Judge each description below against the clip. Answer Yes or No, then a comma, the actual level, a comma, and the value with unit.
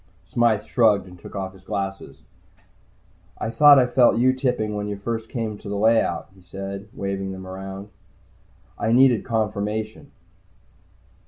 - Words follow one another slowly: No, average, 150 wpm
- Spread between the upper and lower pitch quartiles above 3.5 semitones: No, average, 3.0 semitones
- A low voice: Yes, low, 105 Hz